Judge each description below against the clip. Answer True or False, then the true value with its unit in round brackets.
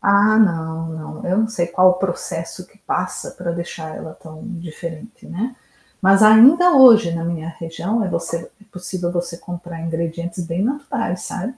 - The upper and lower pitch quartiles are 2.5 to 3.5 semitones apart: False (4.0 semitones)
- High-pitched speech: False (180 Hz)